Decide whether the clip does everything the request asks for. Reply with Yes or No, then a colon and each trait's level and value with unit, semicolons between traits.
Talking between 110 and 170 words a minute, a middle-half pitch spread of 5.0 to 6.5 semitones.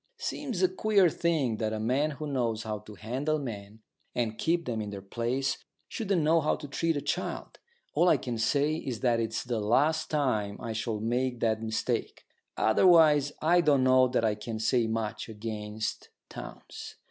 No: average, 180 wpm; wide, 5.5 semitones